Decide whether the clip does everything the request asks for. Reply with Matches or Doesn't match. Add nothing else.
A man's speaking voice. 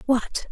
Doesn't match